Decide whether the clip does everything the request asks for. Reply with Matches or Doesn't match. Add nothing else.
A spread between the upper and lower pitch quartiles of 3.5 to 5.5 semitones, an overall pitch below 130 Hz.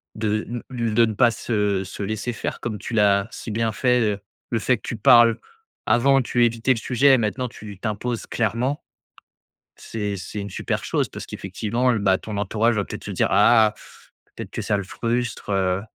Doesn't match